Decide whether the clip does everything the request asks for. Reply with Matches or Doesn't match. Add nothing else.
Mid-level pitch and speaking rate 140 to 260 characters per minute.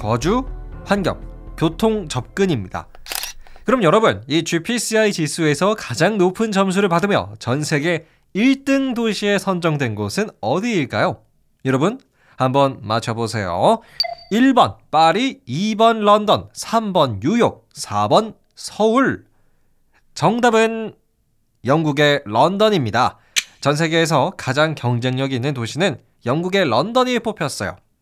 Matches